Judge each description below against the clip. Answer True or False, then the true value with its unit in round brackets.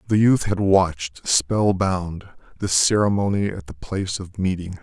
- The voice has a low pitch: True (95 Hz)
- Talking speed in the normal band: True (150 wpm)